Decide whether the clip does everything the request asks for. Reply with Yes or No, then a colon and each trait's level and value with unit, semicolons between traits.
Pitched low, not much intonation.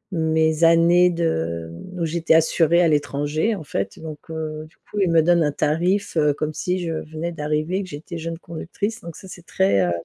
No: medium, 160 Hz; narrow, 2.1 semitones